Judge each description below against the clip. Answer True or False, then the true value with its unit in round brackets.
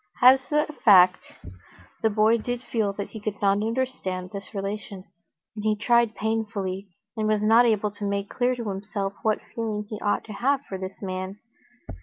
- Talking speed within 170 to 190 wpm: True (180 wpm)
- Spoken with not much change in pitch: True (2.3 semitones)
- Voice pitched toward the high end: True (210 Hz)